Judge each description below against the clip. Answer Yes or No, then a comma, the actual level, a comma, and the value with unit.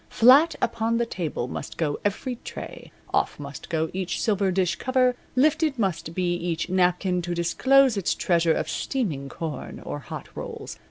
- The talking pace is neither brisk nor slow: Yes, average, 165 wpm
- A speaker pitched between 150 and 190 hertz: Yes, medium, 185 Hz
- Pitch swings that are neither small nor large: No, wide, 6.2 semitones